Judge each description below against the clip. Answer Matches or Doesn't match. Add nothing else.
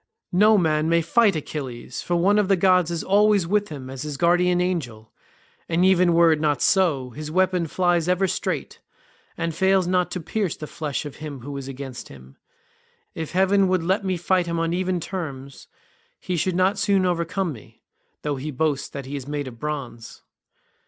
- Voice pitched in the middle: Matches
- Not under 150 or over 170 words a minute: Doesn't match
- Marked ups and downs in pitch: Doesn't match